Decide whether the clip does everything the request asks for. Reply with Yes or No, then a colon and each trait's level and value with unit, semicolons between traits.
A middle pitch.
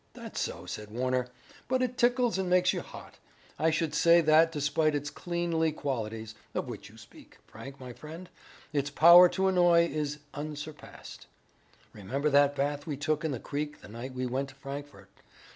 Yes: medium, 150 Hz